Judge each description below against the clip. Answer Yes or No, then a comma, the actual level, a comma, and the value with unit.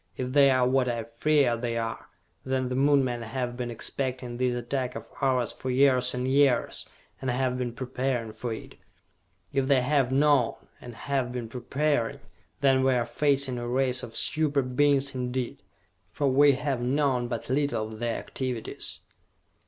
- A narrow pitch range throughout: Yes, narrow, 2.1 semitones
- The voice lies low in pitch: Yes, low, 130 Hz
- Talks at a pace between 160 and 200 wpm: Yes, average, 170 wpm